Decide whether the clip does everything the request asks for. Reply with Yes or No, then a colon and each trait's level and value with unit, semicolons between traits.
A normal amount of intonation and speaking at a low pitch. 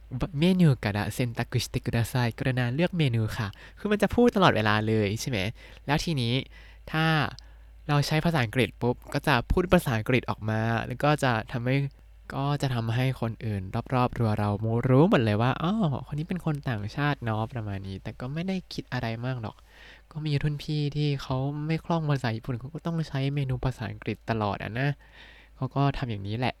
Yes: average, 4.4 semitones; low, 130 Hz